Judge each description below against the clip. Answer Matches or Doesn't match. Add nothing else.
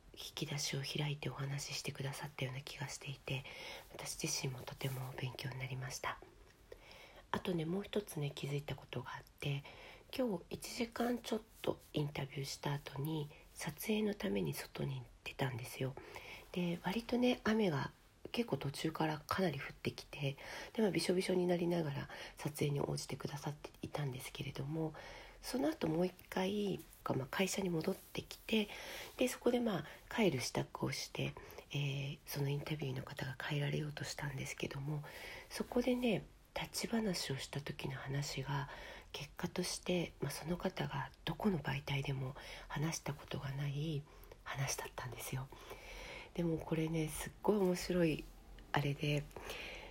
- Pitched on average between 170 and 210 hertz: Doesn't match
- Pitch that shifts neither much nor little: Matches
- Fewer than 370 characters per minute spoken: Matches